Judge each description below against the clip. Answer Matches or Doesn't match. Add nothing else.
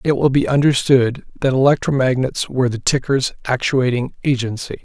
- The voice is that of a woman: Doesn't match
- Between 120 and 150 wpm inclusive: Matches